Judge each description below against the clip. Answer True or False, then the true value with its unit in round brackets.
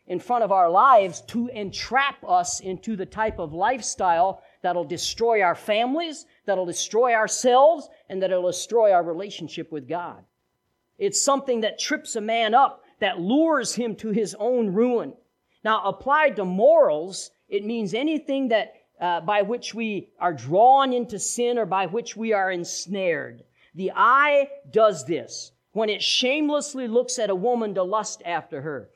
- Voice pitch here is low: False (220 Hz)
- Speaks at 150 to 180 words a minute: True (160 wpm)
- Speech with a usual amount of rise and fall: False (5.8 semitones)